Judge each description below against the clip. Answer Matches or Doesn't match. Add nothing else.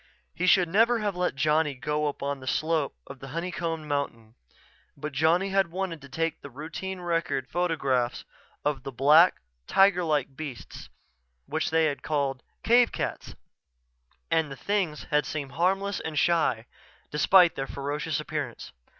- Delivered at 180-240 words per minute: Doesn't match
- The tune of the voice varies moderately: Matches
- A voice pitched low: Doesn't match